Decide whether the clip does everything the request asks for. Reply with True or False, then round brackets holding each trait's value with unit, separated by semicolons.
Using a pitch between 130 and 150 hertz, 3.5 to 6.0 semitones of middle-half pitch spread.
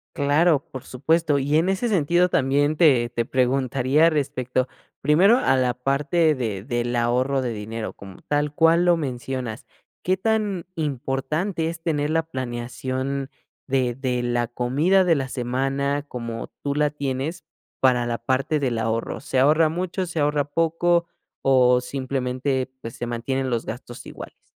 True (135 Hz; 4.0 semitones)